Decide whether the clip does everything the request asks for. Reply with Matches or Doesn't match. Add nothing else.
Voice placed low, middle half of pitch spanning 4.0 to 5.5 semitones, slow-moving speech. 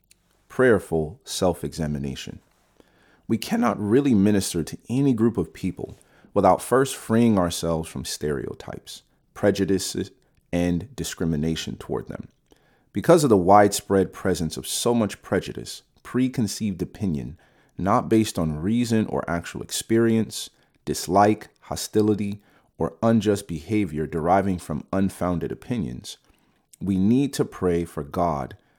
Matches